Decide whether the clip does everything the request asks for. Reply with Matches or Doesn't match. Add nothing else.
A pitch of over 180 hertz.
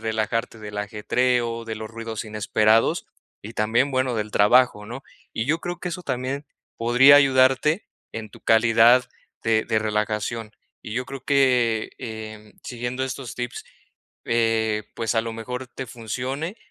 Doesn't match